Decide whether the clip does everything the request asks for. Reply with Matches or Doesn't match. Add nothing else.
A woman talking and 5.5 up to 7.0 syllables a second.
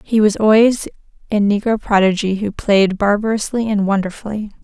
Doesn't match